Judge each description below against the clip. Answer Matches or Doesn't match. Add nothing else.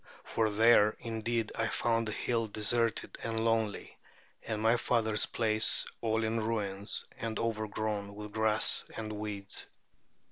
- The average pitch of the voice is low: Matches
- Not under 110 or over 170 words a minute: Matches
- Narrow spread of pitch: Matches